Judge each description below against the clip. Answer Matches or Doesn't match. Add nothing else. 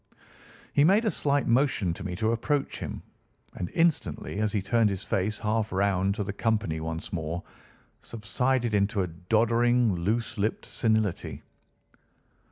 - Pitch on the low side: Matches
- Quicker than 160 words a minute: Doesn't match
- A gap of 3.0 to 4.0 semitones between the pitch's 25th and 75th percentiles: Matches